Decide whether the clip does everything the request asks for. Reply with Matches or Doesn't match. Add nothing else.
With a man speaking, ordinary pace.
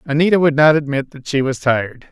Doesn't match